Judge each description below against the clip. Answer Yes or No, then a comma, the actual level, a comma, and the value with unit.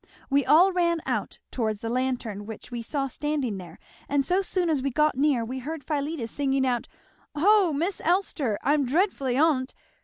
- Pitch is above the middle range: Yes, very high, 280 Hz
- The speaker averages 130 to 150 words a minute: No, average, 180 wpm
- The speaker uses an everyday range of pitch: Yes, average, 4.3 semitones